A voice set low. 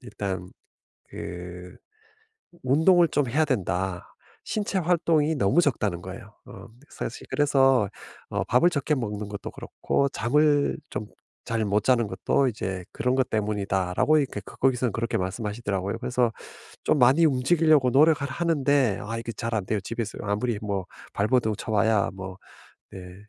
Yes: low, 115 Hz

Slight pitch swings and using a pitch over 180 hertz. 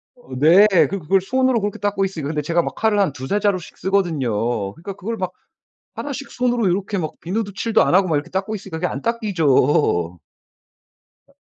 No: average, 5.0 semitones; high, 190 Hz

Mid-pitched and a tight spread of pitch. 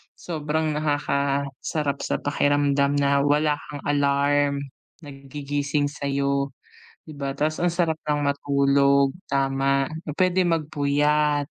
Yes: medium, 145 Hz; narrow, 1.3 semitones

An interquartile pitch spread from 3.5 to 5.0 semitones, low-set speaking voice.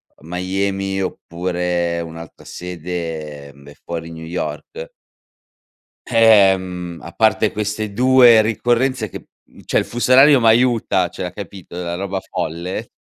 Yes: average, 4.5 semitones; very low, 95 Hz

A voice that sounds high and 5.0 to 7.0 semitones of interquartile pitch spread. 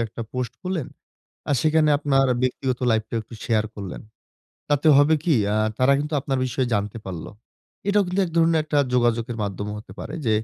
No: low, 130 Hz; average, 5.3 semitones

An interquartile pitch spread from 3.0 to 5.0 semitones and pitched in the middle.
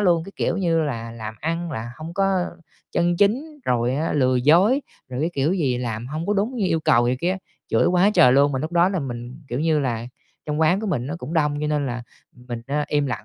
No: wide, 5.6 semitones; medium, 150 Hz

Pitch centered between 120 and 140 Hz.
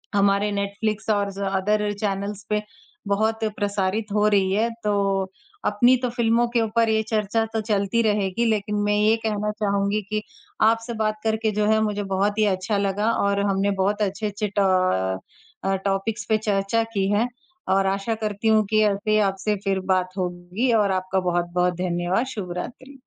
No: high, 205 Hz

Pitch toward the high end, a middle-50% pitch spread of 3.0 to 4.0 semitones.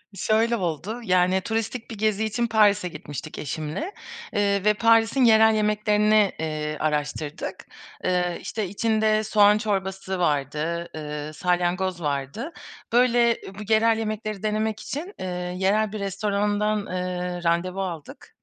Yes: high, 200 Hz; average, 3.6 semitones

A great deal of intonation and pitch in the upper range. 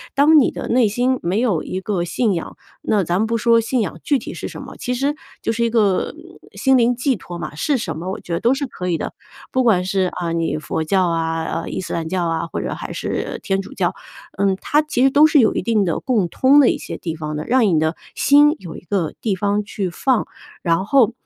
Yes: wide, 6.4 semitones; high, 205 Hz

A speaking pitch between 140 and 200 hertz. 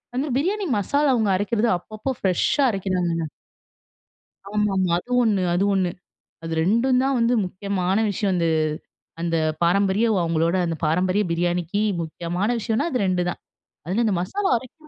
Yes: high, 195 Hz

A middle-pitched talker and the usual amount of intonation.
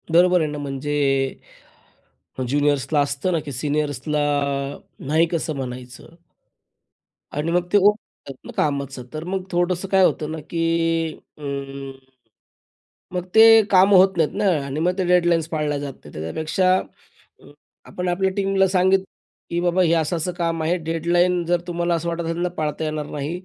Yes: medium, 165 Hz; average, 3.5 semitones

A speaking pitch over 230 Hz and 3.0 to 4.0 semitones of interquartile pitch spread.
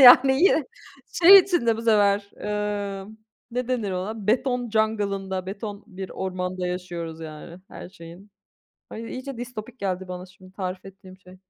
No: high, 200 Hz; average, 3.7 semitones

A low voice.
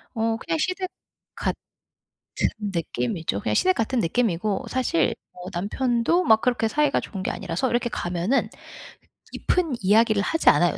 No: high, 225 Hz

